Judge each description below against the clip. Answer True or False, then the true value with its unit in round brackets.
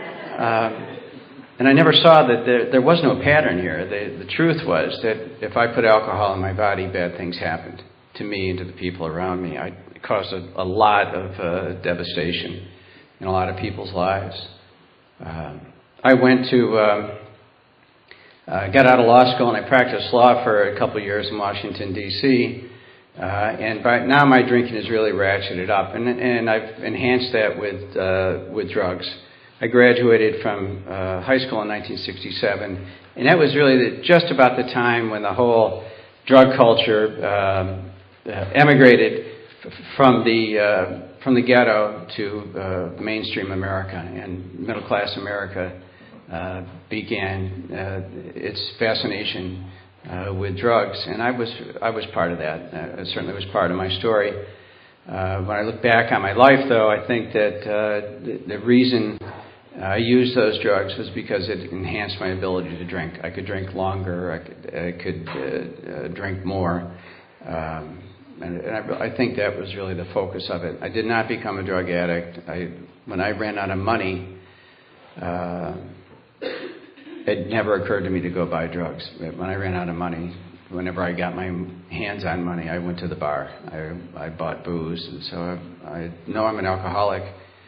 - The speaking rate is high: False (180 wpm)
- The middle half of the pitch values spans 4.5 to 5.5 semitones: False (4.1 semitones)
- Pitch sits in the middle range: False (95 Hz)